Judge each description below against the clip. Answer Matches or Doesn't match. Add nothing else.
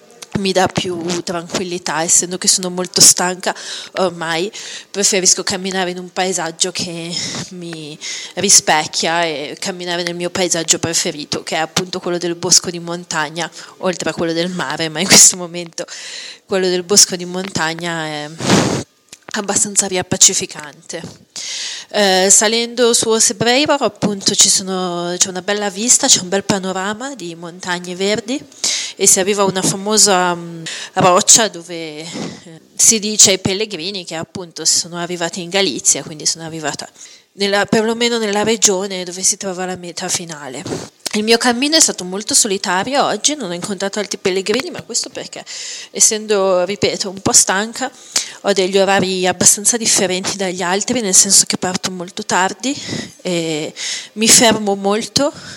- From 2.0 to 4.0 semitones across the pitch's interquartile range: Matches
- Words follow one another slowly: Doesn't match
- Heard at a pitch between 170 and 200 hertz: Matches